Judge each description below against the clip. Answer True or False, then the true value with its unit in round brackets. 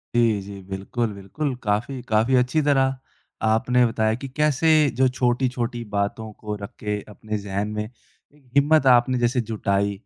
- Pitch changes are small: False (3.8 semitones)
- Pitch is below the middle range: True (120 Hz)